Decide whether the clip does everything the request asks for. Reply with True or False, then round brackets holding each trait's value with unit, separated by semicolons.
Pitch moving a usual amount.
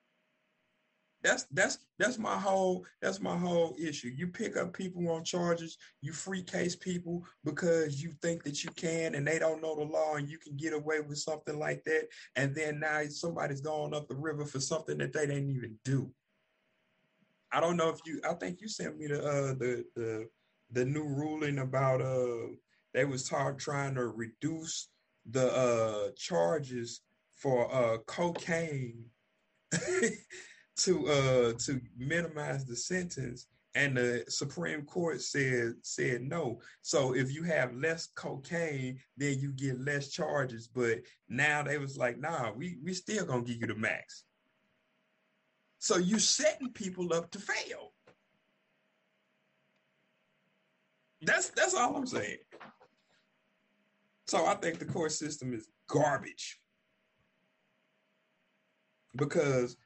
True (4.6 semitones)